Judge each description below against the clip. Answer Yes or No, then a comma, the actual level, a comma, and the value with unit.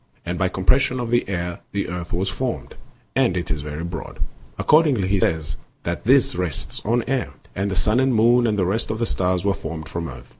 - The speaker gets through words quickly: Yes, fast, 230 wpm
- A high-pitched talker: No, very low, 95 Hz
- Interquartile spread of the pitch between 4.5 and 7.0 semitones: Yes, average, 5.3 semitones